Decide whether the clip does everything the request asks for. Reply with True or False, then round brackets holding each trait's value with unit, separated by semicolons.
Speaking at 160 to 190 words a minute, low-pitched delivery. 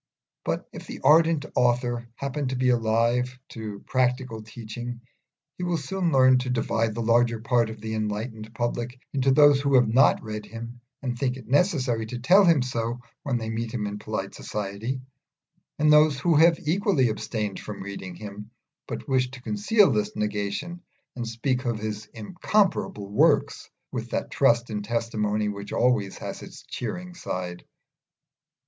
True (165 wpm; 120 Hz)